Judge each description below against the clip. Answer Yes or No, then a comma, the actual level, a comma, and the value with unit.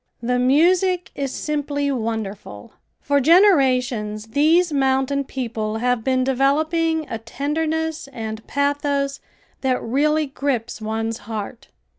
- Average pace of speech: No, slow, 110 wpm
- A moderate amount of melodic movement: Yes, average, 4.6 semitones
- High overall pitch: Yes, very high, 270 Hz